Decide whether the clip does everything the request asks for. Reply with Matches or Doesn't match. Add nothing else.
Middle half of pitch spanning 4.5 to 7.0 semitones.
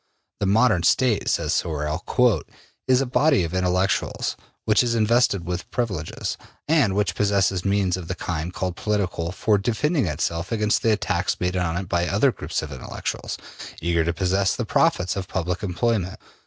Doesn't match